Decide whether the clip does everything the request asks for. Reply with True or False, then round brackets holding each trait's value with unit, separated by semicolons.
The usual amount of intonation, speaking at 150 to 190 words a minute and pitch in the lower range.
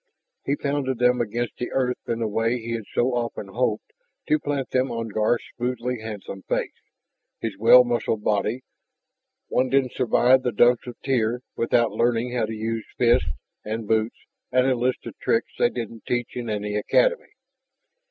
False (2.1 semitones; 170 wpm; 120 Hz)